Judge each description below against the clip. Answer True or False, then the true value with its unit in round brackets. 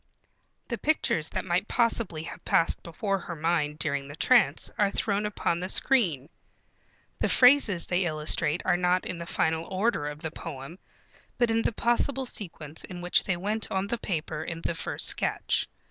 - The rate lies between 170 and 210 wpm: True (175 wpm)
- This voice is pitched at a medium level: True (180 Hz)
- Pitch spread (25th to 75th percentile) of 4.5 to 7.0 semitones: True (4.9 semitones)